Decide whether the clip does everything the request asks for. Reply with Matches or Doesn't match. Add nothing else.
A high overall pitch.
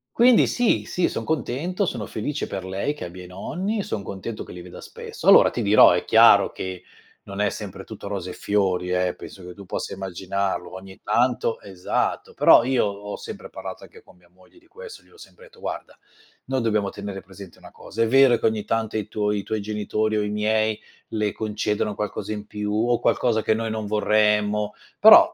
Doesn't match